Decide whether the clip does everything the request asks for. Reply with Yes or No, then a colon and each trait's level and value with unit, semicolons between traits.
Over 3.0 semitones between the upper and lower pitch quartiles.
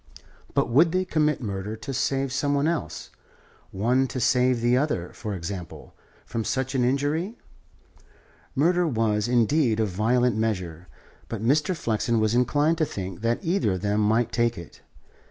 Yes: average, 5.0 semitones